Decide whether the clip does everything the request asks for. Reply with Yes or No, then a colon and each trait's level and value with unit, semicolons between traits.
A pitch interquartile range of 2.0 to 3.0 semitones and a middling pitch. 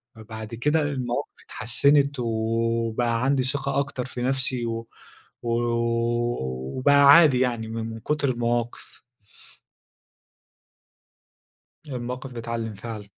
No: narrow, 2.5 semitones; low, 120 Hz